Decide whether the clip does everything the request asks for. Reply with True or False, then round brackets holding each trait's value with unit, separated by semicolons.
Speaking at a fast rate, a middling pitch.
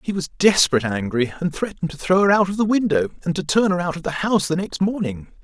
True (265 wpm; 175 Hz)